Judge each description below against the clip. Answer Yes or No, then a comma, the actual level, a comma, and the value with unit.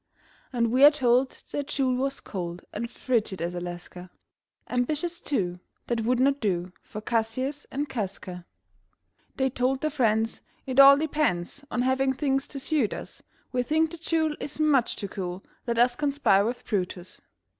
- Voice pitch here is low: No, very high, 250 Hz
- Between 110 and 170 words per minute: Yes, average, 165 wpm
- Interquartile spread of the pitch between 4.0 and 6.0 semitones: Yes, average, 5.1 semitones